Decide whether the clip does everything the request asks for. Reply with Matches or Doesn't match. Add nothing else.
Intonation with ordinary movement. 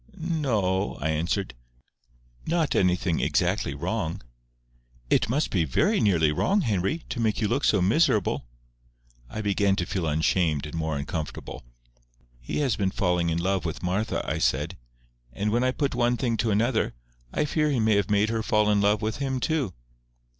Doesn't match